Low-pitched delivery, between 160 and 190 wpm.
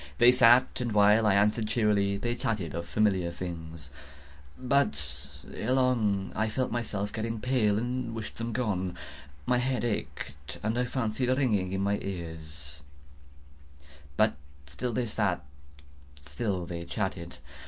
No: low, 105 Hz; average, 145 wpm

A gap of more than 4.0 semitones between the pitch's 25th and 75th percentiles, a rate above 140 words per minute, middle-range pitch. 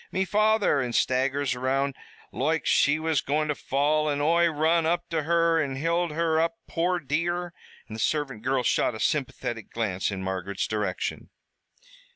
Yes: average, 4.4 semitones; average, 170 wpm; medium, 150 Hz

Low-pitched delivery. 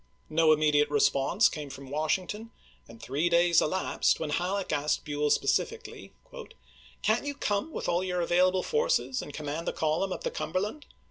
No: medium, 165 Hz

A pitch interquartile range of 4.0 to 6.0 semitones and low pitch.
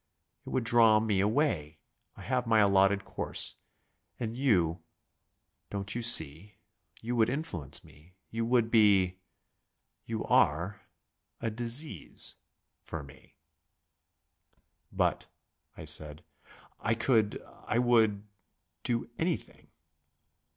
Yes: average, 4.3 semitones; low, 110 Hz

